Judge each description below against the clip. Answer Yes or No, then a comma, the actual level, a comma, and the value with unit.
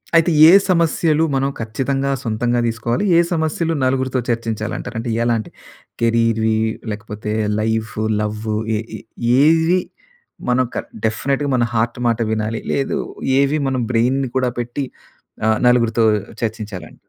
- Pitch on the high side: No, low, 120 Hz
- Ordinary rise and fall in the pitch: Yes, average, 3.6 semitones